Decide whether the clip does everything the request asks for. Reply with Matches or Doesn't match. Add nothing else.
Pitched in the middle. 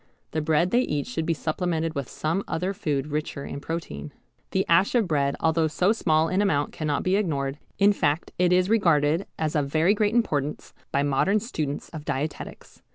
Matches